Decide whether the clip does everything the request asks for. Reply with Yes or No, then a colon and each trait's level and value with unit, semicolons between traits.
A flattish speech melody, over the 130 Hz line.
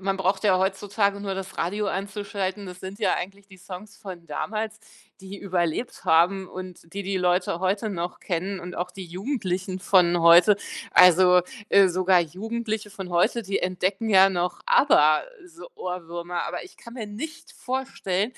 Yes: narrow, 2.2 semitones; high, 190 Hz